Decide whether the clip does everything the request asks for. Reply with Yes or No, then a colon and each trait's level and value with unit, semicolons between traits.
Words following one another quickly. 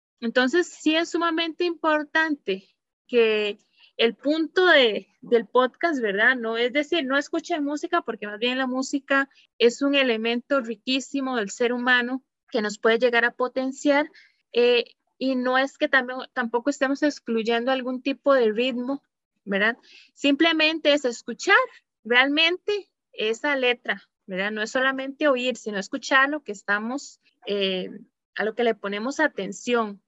No: average, 145 wpm